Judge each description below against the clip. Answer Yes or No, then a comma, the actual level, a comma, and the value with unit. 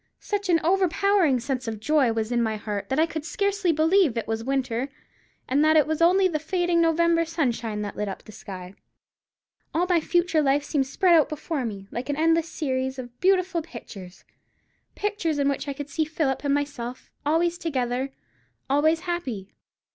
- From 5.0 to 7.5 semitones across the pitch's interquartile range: Yes, average, 5.3 semitones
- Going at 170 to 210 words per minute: Yes, average, 180 wpm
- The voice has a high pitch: Yes, very high, 295 Hz